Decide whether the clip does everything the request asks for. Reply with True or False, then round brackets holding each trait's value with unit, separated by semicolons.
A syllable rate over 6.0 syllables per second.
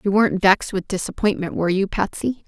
True (6.3 syllables/s)